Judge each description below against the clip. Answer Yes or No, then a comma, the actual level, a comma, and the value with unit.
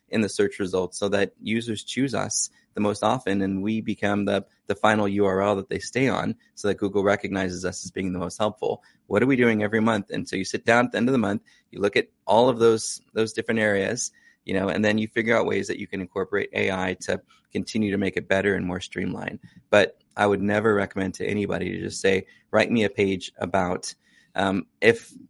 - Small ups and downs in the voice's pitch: Yes, narrow, 2.2 semitones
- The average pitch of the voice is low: Yes, low, 100 Hz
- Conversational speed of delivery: No, fast, 230 wpm